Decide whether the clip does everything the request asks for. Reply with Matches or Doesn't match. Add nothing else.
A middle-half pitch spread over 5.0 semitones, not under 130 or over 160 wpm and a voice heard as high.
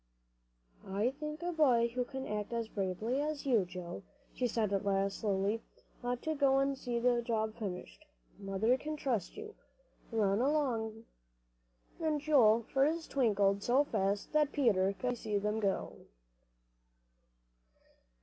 Matches